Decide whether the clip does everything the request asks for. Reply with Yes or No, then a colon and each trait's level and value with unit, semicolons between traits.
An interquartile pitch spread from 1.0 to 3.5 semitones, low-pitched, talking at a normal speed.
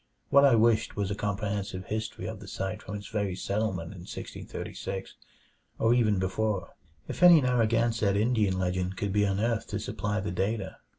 Yes: average, 2.7 semitones; low, 105 Hz; average, 170 wpm